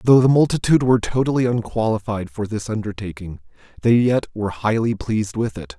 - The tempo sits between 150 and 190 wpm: Yes, average, 165 wpm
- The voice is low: Yes, low, 115 Hz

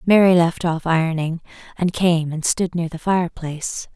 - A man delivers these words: No, female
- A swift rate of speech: No, average, 180 wpm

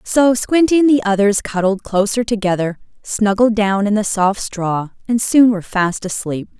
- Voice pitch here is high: Yes, high, 210 Hz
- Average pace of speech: Yes, average, 175 wpm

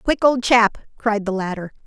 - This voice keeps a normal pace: Yes, average, 195 wpm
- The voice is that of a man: No, female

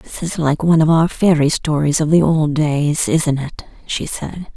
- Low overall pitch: No, medium, 155 Hz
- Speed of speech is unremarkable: No, fast, 210 wpm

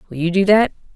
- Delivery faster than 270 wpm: No, fast, 250 wpm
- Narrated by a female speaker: Yes, female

